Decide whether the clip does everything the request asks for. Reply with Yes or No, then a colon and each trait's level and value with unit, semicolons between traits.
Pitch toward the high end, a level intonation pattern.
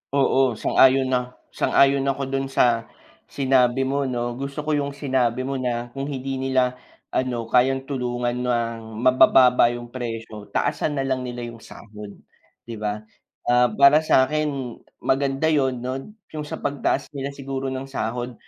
No: low, 130 Hz; narrow, 2.0 semitones